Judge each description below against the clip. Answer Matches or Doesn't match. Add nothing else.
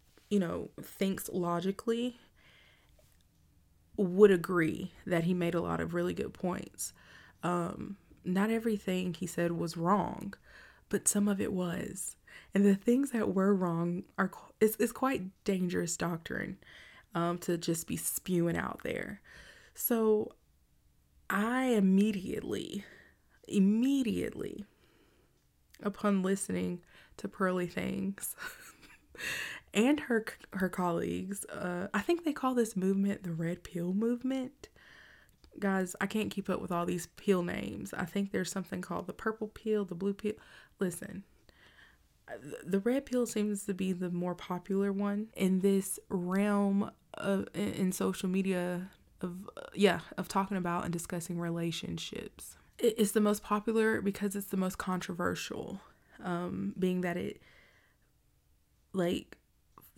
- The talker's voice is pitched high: Matches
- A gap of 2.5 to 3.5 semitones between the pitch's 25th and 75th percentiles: Matches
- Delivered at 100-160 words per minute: Matches